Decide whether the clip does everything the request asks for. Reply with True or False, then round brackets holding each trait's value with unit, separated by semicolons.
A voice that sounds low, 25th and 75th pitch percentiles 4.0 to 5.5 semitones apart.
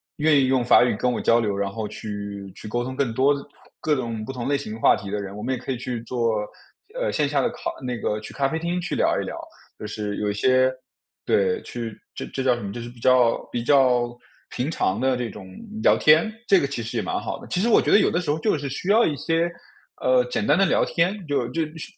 True (125 Hz; 4.6 semitones)